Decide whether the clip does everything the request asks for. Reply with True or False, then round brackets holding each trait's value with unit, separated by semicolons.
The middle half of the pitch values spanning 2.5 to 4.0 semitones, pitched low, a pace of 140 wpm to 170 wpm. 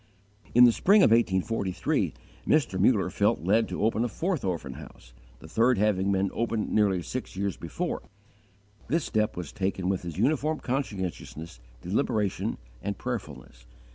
False (4.6 semitones; 100 Hz; 150 wpm)